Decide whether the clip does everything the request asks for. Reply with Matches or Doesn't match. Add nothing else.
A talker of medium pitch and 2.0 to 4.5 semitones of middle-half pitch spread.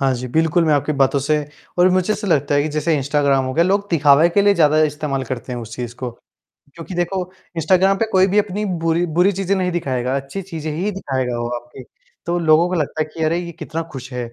Doesn't match